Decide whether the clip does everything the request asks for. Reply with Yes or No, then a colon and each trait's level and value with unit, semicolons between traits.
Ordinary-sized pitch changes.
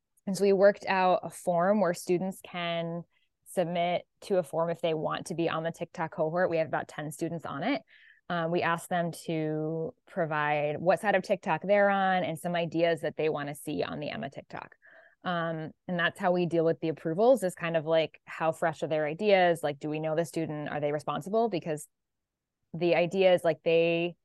No: narrow, 2.3 semitones